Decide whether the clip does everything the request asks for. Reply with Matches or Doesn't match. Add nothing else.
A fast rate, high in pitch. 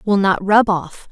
Matches